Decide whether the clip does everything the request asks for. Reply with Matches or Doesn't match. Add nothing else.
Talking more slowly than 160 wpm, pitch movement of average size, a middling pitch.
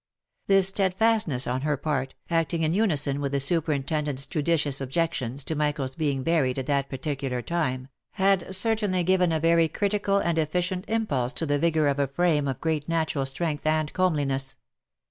Doesn't match